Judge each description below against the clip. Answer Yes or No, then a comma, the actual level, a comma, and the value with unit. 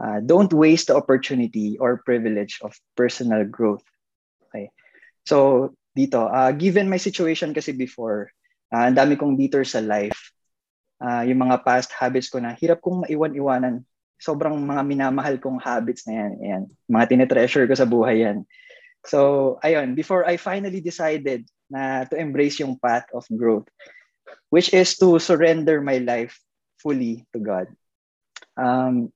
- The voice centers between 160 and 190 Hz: No, low, 135 Hz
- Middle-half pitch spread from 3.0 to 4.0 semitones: No, average, 5.0 semitones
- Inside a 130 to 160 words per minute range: Yes, average, 150 wpm